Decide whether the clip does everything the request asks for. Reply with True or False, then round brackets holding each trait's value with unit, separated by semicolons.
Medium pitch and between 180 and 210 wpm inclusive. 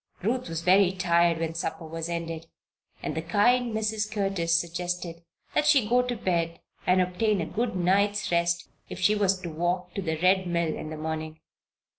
True (180 Hz; 185 wpm)